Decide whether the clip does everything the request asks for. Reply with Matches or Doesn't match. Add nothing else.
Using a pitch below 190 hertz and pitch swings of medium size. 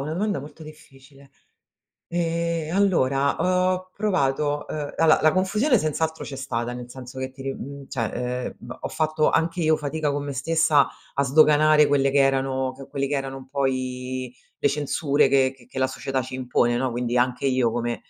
Matches